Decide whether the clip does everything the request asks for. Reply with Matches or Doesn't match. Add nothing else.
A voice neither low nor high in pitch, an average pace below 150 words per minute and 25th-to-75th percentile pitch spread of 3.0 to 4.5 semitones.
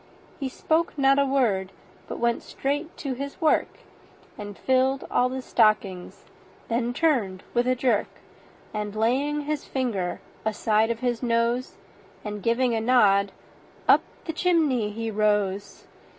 Doesn't match